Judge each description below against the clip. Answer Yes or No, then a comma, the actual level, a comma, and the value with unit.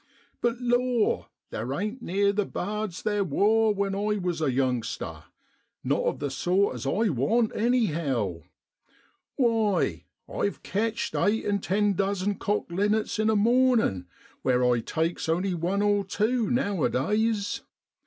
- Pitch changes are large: No, average, 4.6 semitones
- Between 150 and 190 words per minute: No, average, 140 wpm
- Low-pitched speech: No, high, 200 Hz